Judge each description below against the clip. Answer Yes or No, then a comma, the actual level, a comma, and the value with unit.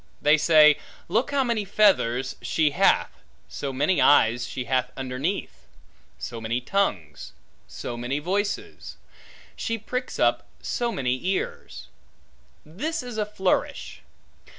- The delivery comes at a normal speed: No, slow, 125 wpm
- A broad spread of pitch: Yes, wide, 8.5 semitones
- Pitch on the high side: No, medium, 155 Hz